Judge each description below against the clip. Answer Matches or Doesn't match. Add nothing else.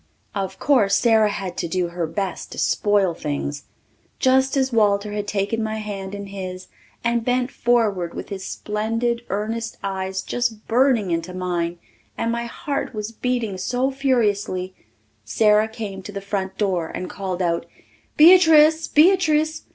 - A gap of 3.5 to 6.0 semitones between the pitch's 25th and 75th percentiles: Matches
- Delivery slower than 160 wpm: Matches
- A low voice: Doesn't match